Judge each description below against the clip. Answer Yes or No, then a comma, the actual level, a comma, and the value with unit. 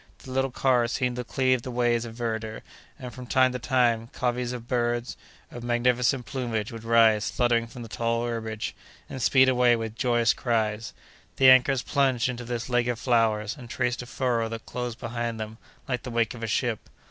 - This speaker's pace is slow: No, average, 195 wpm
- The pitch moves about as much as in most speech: No, narrow, 1.6 semitones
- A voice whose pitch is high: No, low, 120 Hz